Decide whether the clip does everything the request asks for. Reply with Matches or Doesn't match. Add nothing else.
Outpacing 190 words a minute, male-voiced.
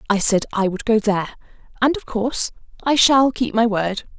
Doesn't match